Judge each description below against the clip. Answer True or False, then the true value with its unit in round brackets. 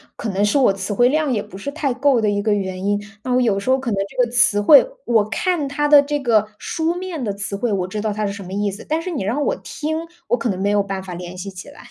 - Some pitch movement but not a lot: False (6.0 semitones)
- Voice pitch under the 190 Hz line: False (220 Hz)